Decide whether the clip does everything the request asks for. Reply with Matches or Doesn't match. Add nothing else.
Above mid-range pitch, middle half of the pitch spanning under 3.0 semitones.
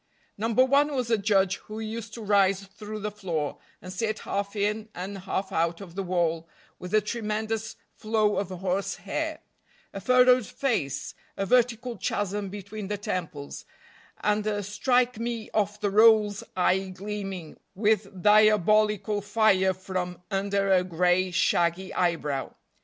Matches